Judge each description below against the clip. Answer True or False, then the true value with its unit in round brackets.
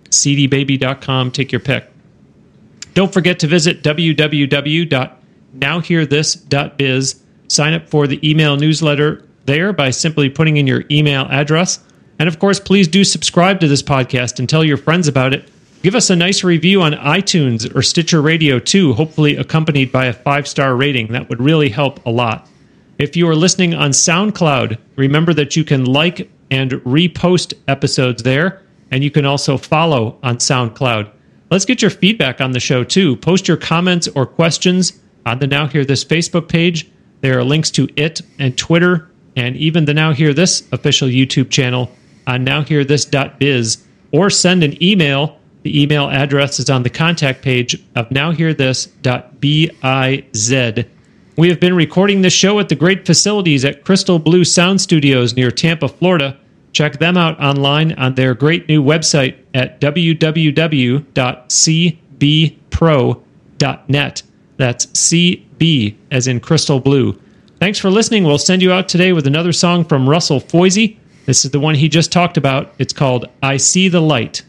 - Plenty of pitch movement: False (4.1 semitones)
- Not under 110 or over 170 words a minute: True (160 wpm)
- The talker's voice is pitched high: False (150 Hz)